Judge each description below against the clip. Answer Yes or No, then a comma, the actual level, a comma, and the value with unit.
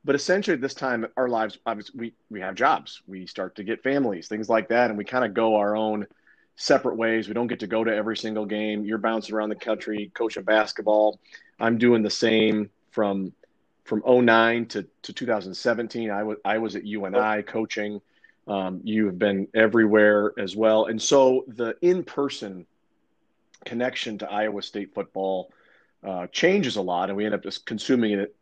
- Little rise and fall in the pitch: Yes, narrow, 1.7 semitones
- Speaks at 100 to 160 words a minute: No, average, 190 wpm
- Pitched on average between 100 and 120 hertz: Yes, low, 110 Hz